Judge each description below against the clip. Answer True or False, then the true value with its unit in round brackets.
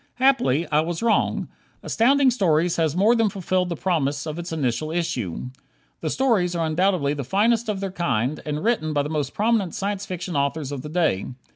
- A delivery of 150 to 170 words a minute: False (190 wpm)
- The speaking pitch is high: False (170 Hz)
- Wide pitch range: False (5.0 semitones)